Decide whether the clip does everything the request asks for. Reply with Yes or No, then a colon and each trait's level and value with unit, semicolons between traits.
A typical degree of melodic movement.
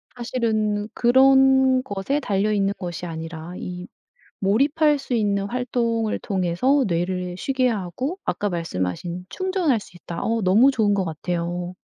No: wide, 6.2 semitones